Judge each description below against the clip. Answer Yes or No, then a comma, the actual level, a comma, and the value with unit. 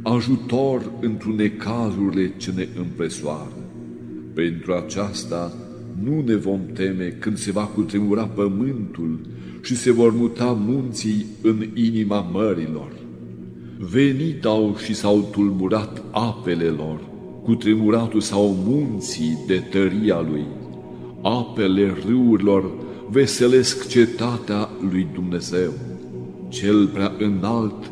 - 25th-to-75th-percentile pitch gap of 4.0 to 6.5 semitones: Yes, average, 5.1 semitones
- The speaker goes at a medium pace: No, slow, 105 wpm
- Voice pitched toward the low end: Yes, low, 100 Hz